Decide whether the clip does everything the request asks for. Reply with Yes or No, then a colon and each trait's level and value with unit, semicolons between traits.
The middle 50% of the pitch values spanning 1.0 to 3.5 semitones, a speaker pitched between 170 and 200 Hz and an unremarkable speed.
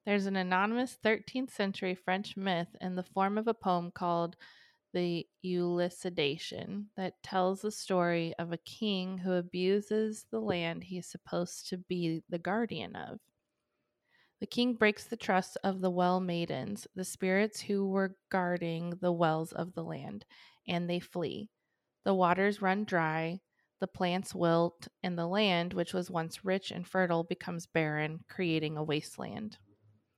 Yes: average, 2.9 semitones; medium, 185 Hz; average, 155 wpm